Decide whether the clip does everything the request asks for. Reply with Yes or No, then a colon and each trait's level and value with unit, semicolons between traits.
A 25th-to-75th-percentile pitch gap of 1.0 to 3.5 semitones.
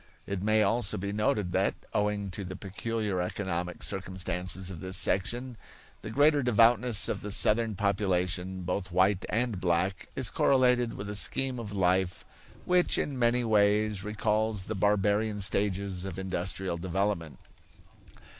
Yes: average, 2.8 semitones